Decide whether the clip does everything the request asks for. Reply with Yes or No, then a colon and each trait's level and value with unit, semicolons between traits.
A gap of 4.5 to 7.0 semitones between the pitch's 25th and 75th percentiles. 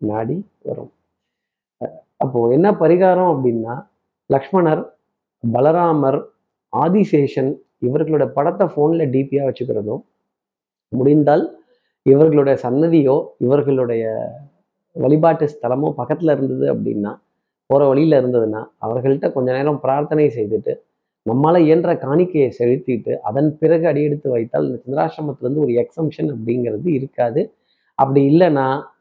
No: average, 3.5 semitones